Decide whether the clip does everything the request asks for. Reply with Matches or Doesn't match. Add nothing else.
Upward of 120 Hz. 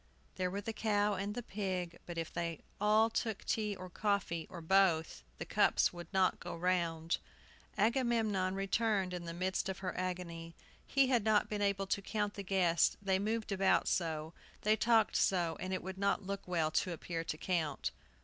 Matches